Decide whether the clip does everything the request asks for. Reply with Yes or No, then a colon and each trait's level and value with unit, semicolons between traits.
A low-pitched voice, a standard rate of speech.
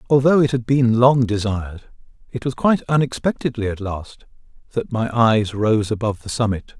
Yes: low, 120 Hz; average, 170 wpm